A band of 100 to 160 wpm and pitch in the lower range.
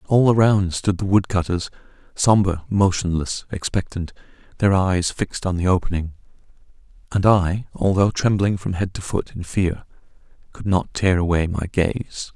Yes: average, 145 wpm; very low, 95 Hz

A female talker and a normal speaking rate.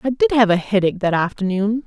No: female; fast, 225 wpm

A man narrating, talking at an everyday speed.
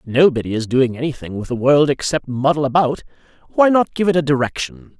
Yes: male; average, 190 wpm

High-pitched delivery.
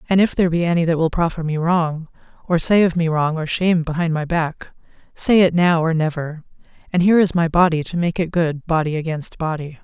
No: medium, 165 Hz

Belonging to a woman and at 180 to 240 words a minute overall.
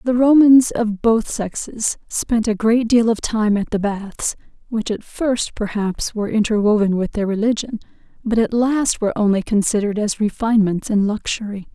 No: female; average, 170 wpm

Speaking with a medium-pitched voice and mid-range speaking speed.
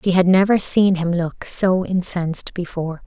Yes: medium, 180 Hz; average, 175 wpm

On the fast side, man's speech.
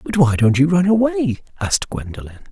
No: average, 190 wpm; male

